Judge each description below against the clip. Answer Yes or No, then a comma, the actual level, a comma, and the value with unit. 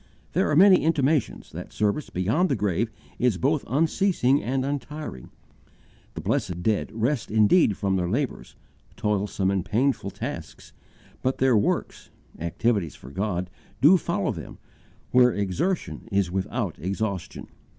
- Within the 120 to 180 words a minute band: Yes, slow, 135 wpm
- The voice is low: Yes, low, 110 Hz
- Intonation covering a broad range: Yes, wide, 6.5 semitones